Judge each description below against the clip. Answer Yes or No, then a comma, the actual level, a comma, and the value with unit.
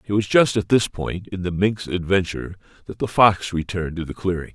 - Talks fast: Yes, fast, 225 wpm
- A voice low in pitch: Yes, very low, 95 Hz